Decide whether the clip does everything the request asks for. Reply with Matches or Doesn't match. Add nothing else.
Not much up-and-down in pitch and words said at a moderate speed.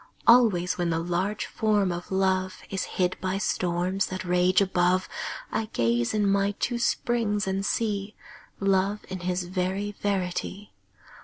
Matches